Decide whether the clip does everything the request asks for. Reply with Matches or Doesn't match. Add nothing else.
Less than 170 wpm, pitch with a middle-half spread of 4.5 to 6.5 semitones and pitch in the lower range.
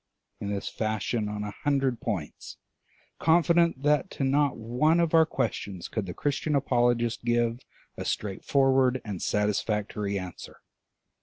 Matches